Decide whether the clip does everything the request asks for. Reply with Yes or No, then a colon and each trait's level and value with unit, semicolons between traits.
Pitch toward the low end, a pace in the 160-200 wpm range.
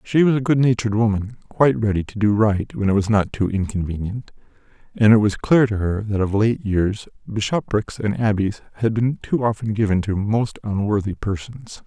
Yes: low, 105 Hz; average, 190 wpm